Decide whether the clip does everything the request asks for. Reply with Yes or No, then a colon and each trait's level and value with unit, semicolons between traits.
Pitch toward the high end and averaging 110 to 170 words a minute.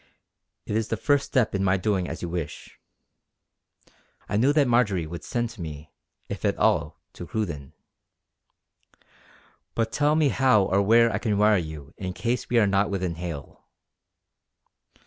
No: low, 100 Hz; average, 165 wpm